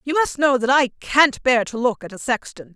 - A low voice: No, very high, 250 Hz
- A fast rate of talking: Yes, fast, 260 wpm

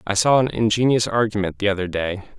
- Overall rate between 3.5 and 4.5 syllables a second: No, 6.0 syllables/s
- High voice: No, low, 105 Hz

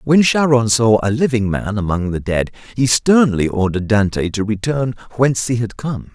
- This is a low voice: Yes, low, 115 Hz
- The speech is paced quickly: No, average, 185 wpm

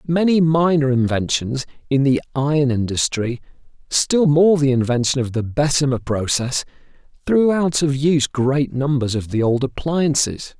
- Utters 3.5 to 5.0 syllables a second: Yes, 4.6 syllables/s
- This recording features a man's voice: Yes, male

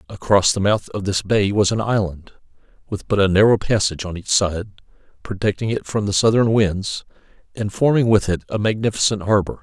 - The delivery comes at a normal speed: Yes, average, 185 wpm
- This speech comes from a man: Yes, male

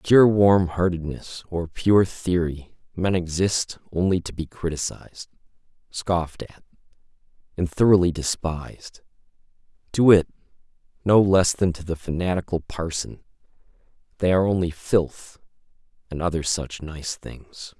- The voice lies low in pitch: Yes, very low, 90 Hz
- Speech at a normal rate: No, slow, 120 wpm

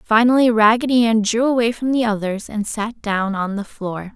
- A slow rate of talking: No, average, 200 wpm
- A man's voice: No, female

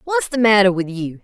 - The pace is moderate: No, fast, 240 wpm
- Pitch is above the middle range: Yes, high, 215 Hz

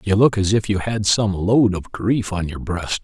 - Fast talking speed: Yes, fast, 255 wpm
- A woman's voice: No, male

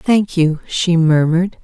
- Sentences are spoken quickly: No, average, 145 wpm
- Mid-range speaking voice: Yes, medium, 170 Hz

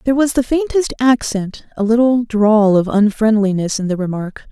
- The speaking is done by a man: No, female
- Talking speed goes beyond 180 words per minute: No, average, 175 wpm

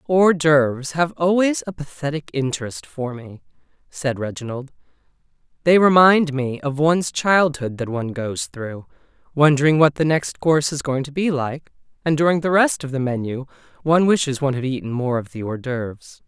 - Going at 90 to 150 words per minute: No, average, 175 wpm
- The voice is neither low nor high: Yes, medium, 145 Hz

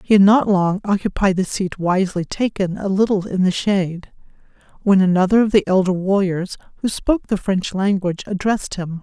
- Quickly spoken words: No, average, 180 wpm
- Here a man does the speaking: No, female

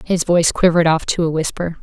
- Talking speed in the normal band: No, fast, 230 wpm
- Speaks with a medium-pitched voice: Yes, medium, 165 Hz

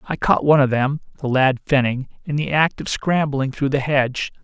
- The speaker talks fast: No, average, 190 wpm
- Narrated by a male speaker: Yes, male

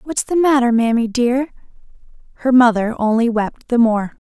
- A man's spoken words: No, female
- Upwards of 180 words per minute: No, average, 155 wpm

